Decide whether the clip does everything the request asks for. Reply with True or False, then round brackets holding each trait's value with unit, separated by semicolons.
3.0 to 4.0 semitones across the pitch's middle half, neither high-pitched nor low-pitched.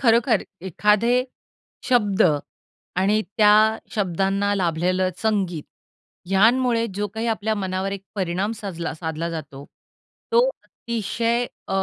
False (3.4 semitones; 205 Hz)